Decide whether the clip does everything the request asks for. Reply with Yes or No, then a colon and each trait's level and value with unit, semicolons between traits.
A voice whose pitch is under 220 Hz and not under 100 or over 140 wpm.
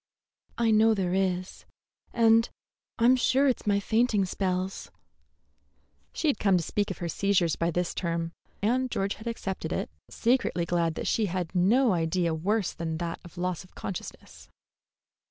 No: high, 190 Hz; average, 160 wpm